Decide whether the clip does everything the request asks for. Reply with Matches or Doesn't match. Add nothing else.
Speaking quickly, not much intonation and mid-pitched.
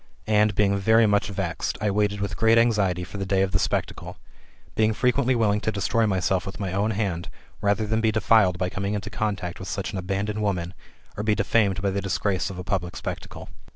Doesn't match